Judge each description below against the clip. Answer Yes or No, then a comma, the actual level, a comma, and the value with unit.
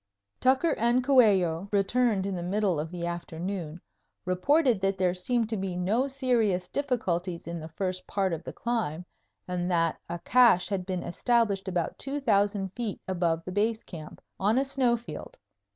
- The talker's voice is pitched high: Yes, high, 195 Hz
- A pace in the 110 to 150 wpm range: No, average, 170 wpm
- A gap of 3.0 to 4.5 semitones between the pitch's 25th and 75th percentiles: No, average, 5.1 semitones